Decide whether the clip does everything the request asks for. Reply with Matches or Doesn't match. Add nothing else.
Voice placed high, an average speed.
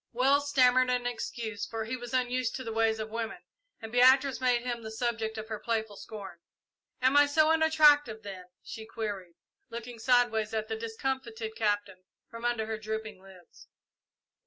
Matches